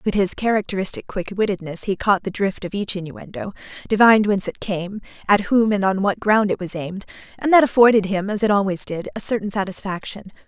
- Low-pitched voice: No, high, 200 Hz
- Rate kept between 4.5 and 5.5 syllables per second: No, 6.0 syllables/s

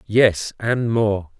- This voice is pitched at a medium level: No, low, 110 Hz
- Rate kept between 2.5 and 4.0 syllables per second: Yes, 2.6 syllables/s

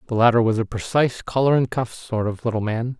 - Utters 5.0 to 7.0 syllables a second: Yes, 6.1 syllables/s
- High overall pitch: No, low, 120 Hz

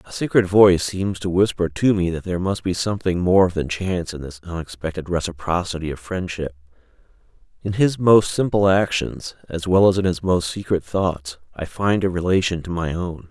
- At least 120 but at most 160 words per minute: No, average, 190 wpm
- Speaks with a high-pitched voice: No, very low, 90 Hz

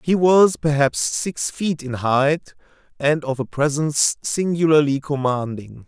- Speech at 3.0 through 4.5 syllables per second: Yes, 4.0 syllables/s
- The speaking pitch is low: No, medium, 145 Hz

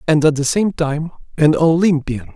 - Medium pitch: Yes, medium, 155 Hz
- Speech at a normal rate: Yes, average, 180 wpm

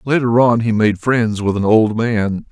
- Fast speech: Yes, fast, 215 wpm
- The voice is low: Yes, low, 110 Hz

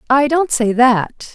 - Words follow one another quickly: No, average, 180 wpm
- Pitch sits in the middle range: No, very high, 255 Hz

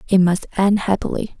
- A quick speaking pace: No, average, 170 wpm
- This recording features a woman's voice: Yes, female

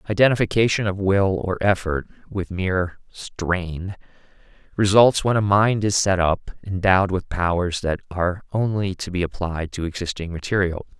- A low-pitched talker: Yes, very low, 95 Hz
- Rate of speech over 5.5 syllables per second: No, 4.9 syllables/s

